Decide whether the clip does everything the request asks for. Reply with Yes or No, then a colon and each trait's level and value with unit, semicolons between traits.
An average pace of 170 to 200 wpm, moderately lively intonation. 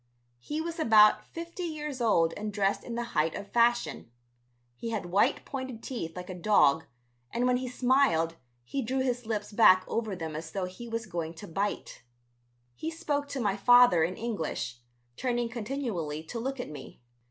No: average, 180 wpm; wide, 6.1 semitones